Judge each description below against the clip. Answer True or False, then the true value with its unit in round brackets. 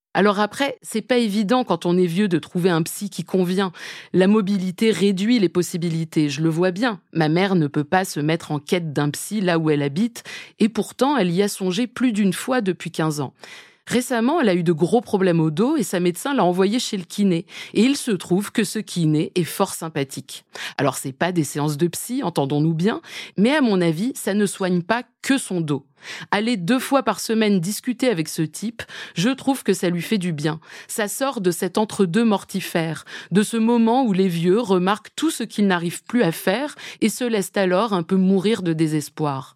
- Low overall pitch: False (190 Hz)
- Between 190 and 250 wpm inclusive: True (220 wpm)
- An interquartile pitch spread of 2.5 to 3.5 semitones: False (4.7 semitones)